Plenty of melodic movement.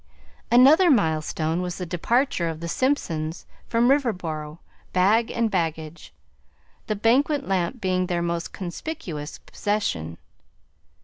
Yes: wide, 6.4 semitones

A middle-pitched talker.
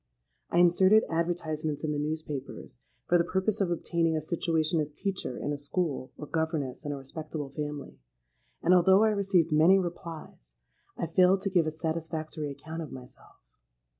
Yes: medium, 160 Hz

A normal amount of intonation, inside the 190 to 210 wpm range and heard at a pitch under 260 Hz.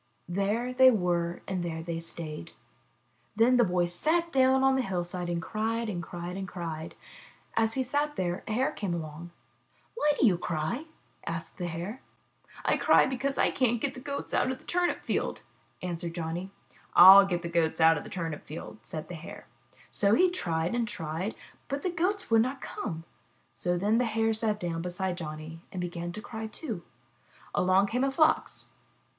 No: wide, 6.4 semitones; average, 195 wpm; high, 190 Hz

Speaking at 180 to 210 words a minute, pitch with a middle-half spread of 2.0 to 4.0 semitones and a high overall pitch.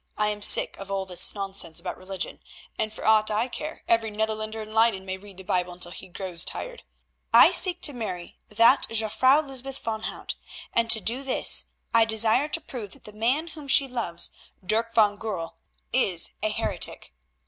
Yes: average, 190 wpm; average, 3.3 semitones; high, 220 Hz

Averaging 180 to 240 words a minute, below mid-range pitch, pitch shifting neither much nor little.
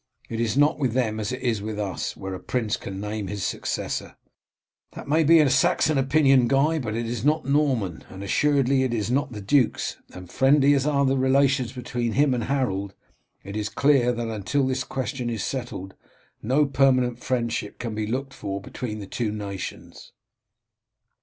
Yes: average, 185 wpm; low, 125 Hz; average, 4.1 semitones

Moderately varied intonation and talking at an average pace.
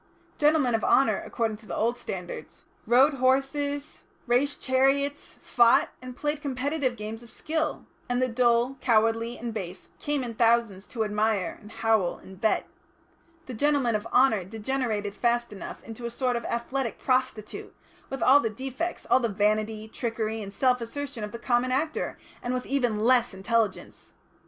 Yes: average, 3.3 semitones; average, 165 wpm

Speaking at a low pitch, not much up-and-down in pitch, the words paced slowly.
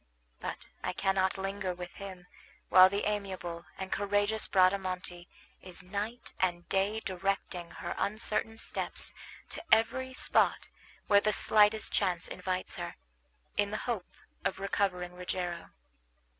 No: high, 195 Hz; narrow, 2.1 semitones; slow, 130 wpm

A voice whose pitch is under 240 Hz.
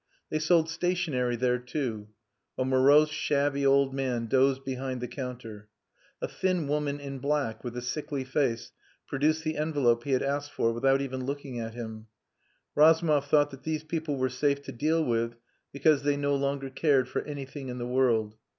Yes: low, 135 Hz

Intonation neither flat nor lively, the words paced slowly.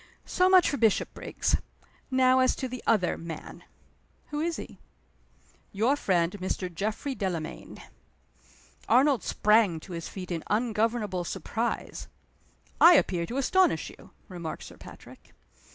No: wide, 6.2 semitones; slow, 130 wpm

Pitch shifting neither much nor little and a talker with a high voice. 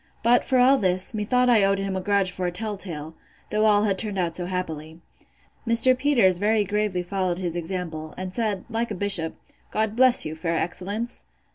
Yes: average, 3.5 semitones; high, 195 Hz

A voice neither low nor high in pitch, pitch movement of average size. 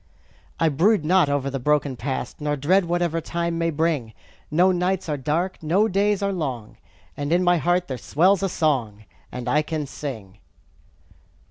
Yes: medium, 160 Hz; average, 4.1 semitones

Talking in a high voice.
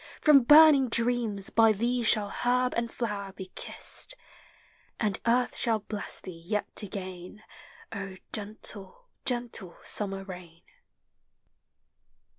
Yes: high, 215 Hz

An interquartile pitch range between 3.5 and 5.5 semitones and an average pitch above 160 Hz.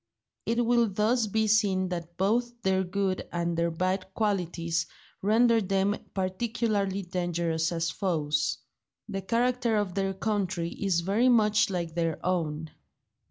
Yes: average, 3.9 semitones; high, 190 Hz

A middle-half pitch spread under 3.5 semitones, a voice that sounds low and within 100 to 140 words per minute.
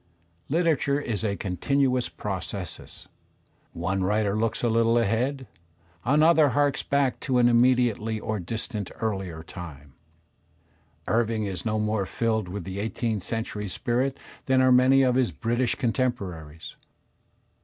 No: average, 4.2 semitones; low, 115 Hz; slow, 135 wpm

